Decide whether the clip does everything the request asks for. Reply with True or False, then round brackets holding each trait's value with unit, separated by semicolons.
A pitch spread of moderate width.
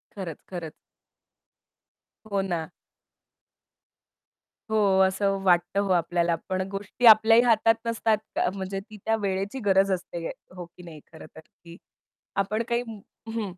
True (3.4 semitones)